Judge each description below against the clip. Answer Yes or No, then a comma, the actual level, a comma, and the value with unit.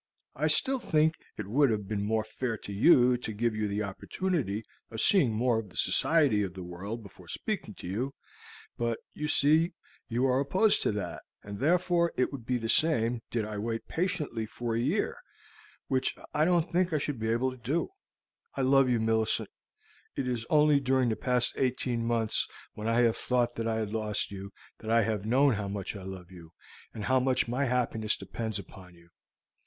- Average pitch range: Yes, average, 4.1 semitones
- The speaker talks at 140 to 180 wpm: No, average, 200 wpm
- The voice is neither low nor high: No, low, 115 Hz